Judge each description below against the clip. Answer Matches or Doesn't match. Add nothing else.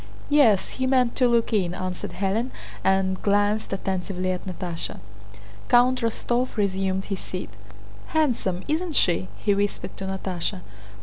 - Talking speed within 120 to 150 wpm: Matches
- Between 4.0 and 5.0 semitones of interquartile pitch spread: Matches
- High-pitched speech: Matches